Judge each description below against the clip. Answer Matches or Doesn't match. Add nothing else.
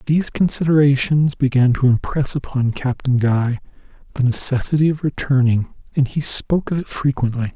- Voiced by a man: Matches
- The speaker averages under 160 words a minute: Matches